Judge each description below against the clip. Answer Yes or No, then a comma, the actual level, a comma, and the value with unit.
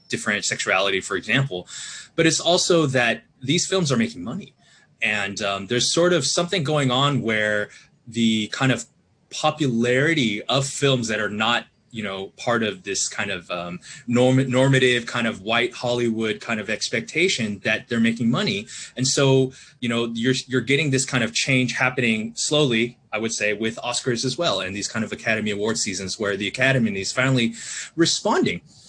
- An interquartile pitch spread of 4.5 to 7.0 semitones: No, average, 3.5 semitones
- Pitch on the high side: No, low, 120 Hz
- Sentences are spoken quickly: No, average, 175 wpm